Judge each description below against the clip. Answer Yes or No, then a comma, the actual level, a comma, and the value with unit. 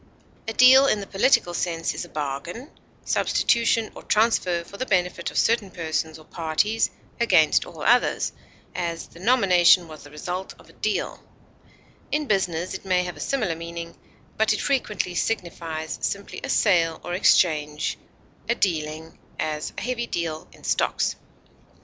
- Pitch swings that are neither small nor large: Yes, average, 4.9 semitones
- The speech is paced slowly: No, average, 155 wpm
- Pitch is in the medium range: Yes, medium, 180 Hz